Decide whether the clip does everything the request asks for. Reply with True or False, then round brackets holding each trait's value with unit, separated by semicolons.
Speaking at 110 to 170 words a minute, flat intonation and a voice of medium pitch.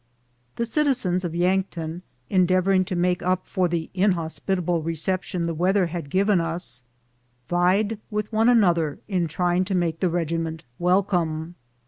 True (140 wpm; 2.3 semitones; 180 Hz)